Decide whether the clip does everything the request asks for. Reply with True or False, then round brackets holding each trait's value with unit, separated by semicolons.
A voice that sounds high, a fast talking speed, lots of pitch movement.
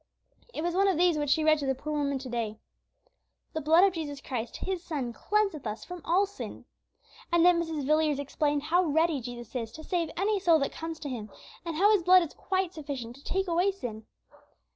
False (315 Hz; 220 wpm; 4.4 semitones)